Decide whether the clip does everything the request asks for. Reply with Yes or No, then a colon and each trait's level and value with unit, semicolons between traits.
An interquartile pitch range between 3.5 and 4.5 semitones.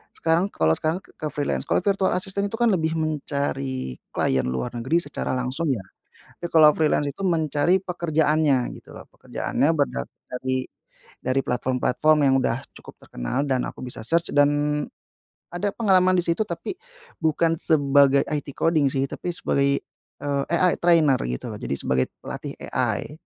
Yes: average, 4.0 semitones